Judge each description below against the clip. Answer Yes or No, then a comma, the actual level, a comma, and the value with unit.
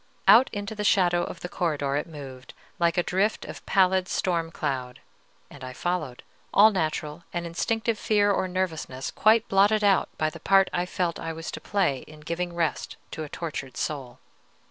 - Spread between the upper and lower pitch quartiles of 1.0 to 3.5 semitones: No, average, 4.3 semitones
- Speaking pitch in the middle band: Yes, medium, 175 Hz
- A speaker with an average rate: Yes, average, 185 wpm